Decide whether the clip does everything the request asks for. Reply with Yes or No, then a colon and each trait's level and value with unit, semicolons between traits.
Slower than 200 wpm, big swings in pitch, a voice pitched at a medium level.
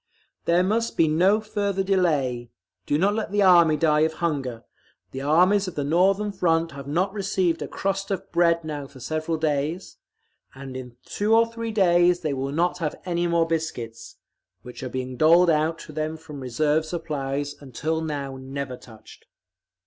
No: average, 170 wpm; average, 4.4 semitones; medium, 160 Hz